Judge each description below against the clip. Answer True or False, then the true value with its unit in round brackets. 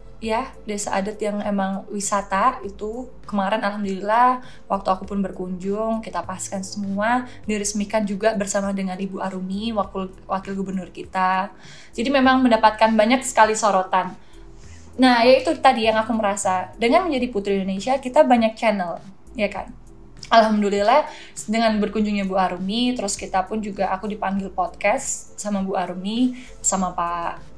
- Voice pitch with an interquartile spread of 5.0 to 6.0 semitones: False (2.6 semitones)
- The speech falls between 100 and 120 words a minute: False (140 wpm)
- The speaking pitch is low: False (205 Hz)